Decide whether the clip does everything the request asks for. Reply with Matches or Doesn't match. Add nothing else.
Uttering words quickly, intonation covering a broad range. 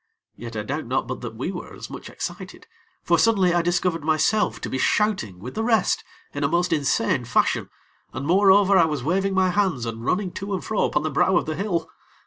Matches